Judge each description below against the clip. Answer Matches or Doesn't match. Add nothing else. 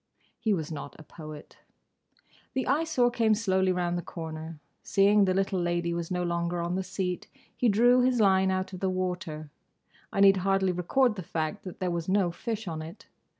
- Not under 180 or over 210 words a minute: Matches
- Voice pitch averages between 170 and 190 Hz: Matches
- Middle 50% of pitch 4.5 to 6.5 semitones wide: Doesn't match